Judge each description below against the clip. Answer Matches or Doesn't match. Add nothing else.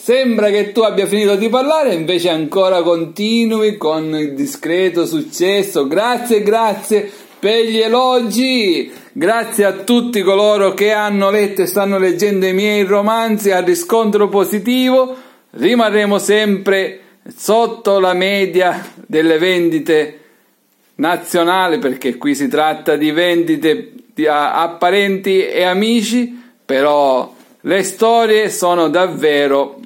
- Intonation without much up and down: Doesn't match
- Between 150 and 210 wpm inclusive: Doesn't match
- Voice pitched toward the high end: Matches